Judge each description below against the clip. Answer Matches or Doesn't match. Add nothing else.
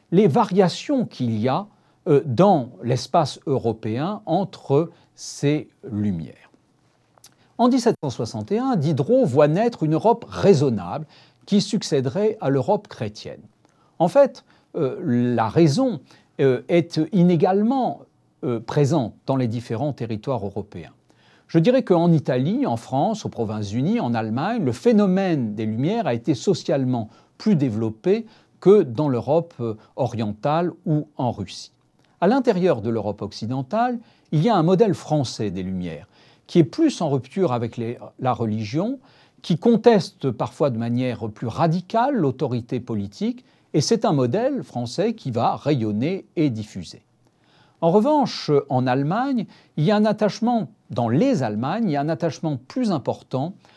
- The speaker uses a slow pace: Matches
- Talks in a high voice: Doesn't match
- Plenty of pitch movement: Matches